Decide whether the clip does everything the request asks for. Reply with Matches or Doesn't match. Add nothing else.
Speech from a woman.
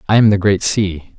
Doesn't match